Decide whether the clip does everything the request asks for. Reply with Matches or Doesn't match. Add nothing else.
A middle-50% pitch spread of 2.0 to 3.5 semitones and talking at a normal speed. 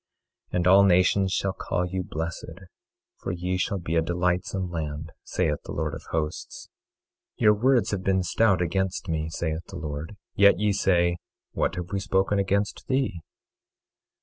Matches